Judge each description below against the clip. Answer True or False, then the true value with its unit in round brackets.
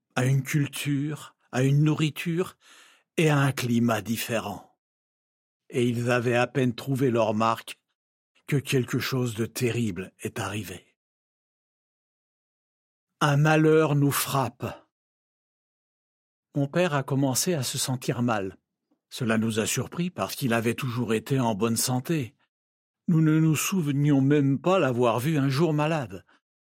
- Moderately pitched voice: False (130 Hz)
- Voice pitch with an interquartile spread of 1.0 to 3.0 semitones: False (4.3 semitones)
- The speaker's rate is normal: False (135 wpm)